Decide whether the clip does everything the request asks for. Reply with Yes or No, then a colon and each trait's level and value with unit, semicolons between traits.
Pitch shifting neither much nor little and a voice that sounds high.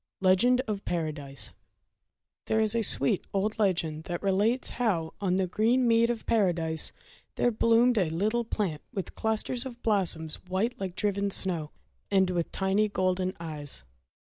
Yes: average, 4.4 semitones; high, 195 Hz